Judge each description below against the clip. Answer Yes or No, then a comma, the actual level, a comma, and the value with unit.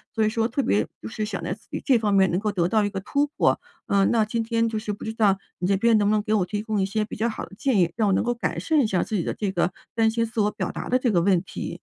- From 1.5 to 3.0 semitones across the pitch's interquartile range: Yes, average, 2.7 semitones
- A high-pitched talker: Yes, high, 215 Hz